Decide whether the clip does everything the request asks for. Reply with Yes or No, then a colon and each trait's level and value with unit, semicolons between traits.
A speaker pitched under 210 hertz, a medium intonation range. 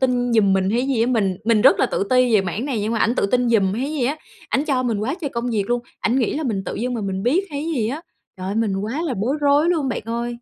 No: high, 240 Hz; average, 3.8 semitones